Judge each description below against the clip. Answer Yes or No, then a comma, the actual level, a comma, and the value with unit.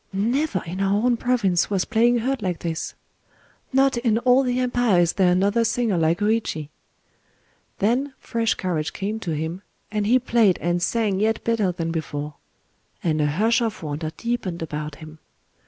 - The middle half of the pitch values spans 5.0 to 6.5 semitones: Yes, wide, 5.6 semitones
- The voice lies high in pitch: Yes, high, 205 Hz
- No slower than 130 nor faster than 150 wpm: No, average, 165 wpm